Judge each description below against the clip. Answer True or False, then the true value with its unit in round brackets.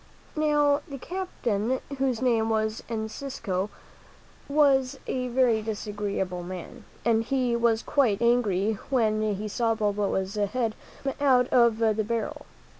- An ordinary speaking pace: False (125 wpm)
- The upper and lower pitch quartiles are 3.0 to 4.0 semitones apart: True (3.4 semitones)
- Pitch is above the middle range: True (230 Hz)